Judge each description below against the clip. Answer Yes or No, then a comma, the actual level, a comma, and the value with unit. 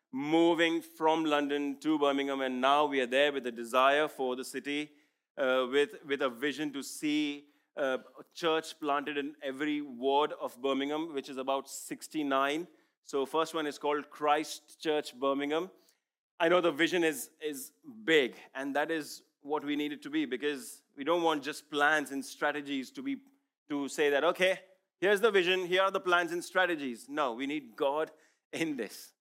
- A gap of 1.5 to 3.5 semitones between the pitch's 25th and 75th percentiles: Yes, average, 3.2 semitones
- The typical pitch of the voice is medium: Yes, medium, 150 Hz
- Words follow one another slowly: No, average, 185 wpm